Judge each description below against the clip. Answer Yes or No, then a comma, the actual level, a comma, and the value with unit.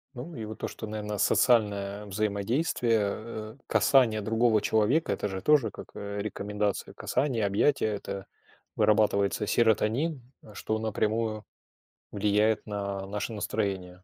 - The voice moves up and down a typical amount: No, narrow, 1.8 semitones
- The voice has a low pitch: Yes, low, 105 Hz